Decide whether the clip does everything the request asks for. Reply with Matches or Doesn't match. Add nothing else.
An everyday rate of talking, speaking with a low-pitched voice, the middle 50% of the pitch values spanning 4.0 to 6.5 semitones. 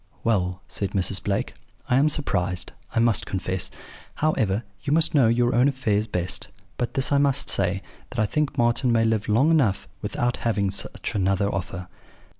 Matches